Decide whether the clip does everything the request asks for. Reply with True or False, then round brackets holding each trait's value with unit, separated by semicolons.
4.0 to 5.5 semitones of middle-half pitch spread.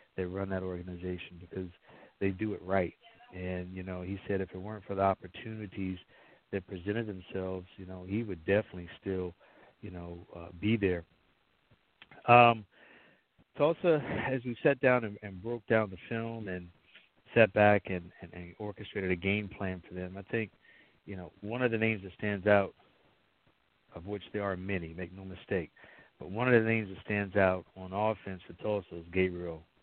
False (2.6 semitones)